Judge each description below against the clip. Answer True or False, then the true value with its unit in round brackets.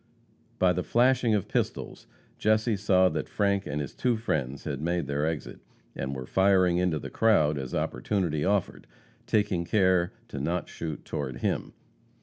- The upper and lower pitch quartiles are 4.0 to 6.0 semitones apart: True (5.4 semitones)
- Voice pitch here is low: True (90 Hz)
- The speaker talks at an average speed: True (160 wpm)